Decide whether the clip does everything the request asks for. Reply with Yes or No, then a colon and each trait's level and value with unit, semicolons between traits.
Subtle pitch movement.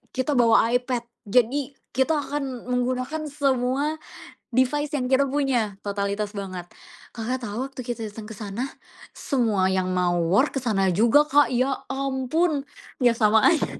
No: average, 4.4 semitones